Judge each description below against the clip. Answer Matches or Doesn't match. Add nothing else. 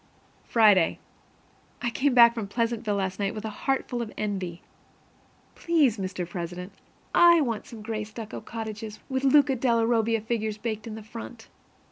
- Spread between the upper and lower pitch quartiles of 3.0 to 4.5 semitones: Doesn't match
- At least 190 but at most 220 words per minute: Doesn't match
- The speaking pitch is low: Doesn't match